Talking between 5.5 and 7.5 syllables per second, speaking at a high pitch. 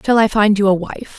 Yes: 5.6 syllables/s; high, 205 Hz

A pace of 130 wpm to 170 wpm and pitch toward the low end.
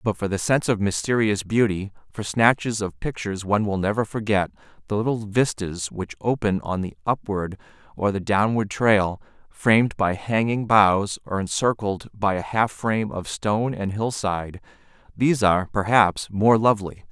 Yes: average, 160 wpm; low, 105 Hz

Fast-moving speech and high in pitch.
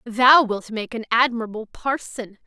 No: average, 145 wpm; high, 235 Hz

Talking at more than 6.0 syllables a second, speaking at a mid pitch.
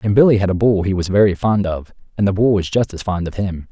No: 6.2 syllables/s; low, 100 Hz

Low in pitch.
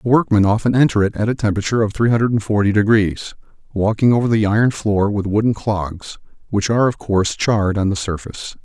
Yes: low, 105 Hz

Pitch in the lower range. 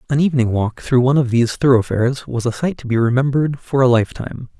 Yes: low, 125 Hz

